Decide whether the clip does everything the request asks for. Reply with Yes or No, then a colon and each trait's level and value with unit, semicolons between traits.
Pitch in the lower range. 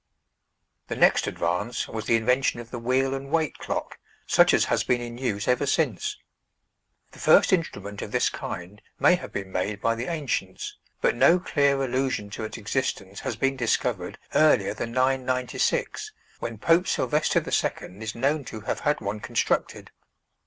Yes: low, 125 Hz